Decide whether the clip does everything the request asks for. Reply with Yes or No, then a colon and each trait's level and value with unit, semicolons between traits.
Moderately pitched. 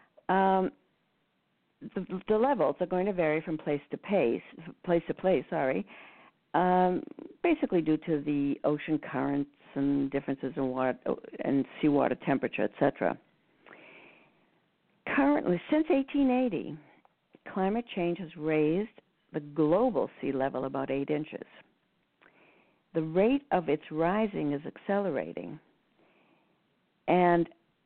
Yes: medium, 170 Hz